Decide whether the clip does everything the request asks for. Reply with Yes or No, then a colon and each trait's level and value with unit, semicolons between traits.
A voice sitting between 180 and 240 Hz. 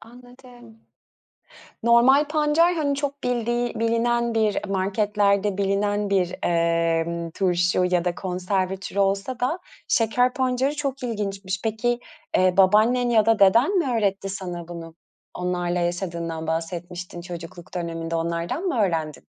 Yes: high, 200 Hz